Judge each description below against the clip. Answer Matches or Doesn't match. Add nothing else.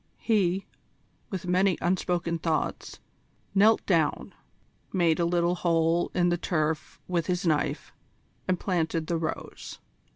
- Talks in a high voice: Doesn't match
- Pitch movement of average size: Doesn't match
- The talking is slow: Matches